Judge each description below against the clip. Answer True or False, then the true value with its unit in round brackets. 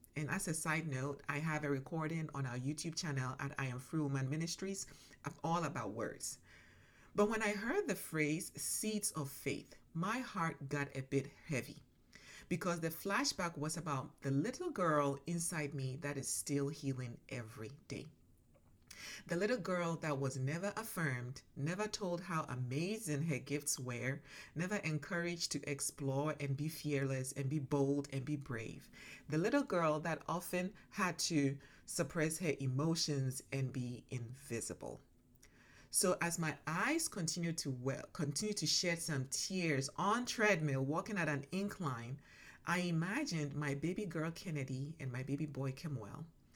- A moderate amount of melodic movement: True (3.6 semitones)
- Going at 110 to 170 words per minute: True (160 wpm)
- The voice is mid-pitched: True (150 Hz)